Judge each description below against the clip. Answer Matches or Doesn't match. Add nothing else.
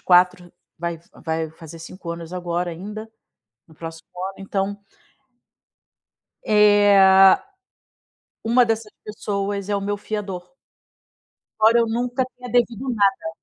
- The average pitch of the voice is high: Matches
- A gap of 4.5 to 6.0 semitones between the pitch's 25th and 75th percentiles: Doesn't match